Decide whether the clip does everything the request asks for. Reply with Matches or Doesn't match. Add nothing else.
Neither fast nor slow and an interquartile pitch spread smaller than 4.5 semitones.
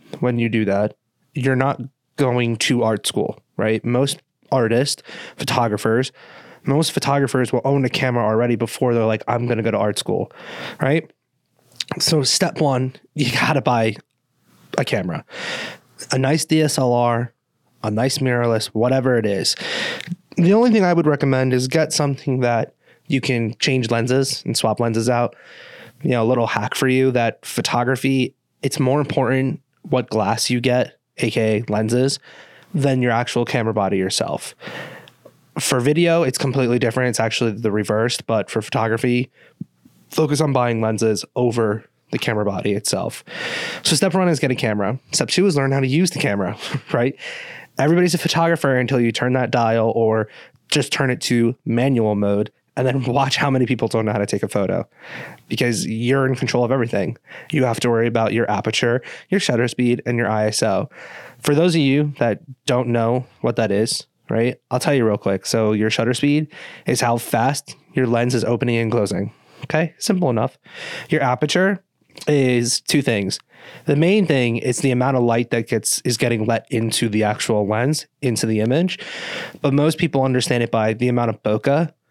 Matches